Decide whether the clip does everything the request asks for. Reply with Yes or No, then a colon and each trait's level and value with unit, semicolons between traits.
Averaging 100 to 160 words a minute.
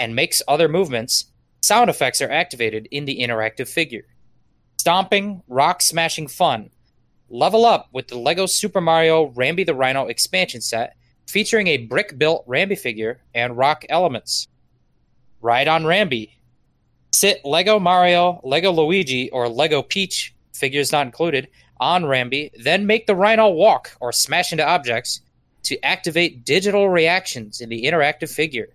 Yes: average, 145 wpm